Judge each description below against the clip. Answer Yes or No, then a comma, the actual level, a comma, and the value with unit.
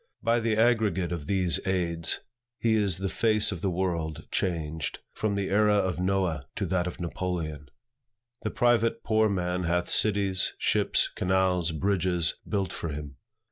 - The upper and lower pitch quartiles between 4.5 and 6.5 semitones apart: No, average, 3.1 semitones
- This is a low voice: Yes, very low, 95 Hz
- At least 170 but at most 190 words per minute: No, average, 155 wpm